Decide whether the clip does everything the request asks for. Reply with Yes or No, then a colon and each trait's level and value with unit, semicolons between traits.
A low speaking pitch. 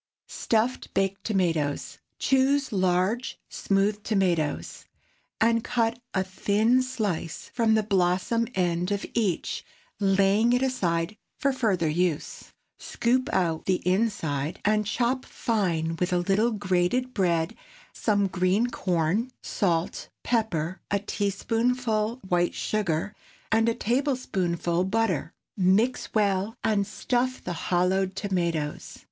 No: high, 200 Hz